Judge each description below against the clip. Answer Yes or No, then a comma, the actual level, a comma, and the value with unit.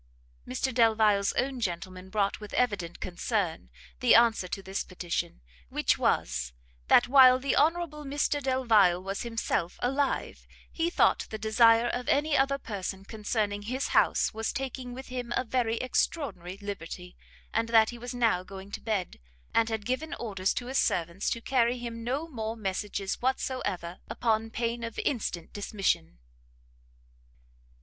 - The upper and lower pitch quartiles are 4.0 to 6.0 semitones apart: Yes, average, 4.5 semitones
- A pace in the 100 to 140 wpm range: No, average, 150 wpm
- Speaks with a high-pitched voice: Yes, high, 225 Hz